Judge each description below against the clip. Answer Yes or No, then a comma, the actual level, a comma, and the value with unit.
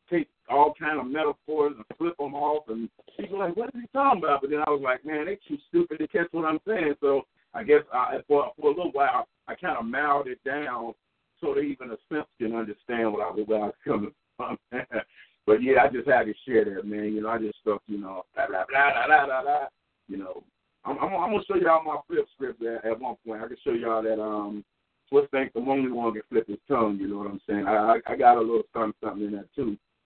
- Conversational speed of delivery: No, fast, 250 wpm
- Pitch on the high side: No, medium, 140 Hz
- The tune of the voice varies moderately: No, wide, 7.2 semitones